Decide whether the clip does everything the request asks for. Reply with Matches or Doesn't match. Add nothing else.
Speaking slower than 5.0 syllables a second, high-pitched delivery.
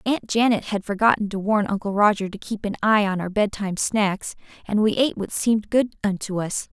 Doesn't match